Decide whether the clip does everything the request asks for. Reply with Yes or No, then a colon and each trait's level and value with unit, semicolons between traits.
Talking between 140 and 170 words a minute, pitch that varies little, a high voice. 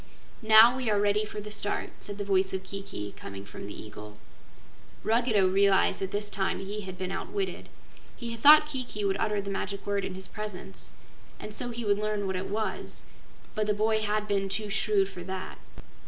No: average, 200 wpm; narrow, 2.0 semitones; high, 205 Hz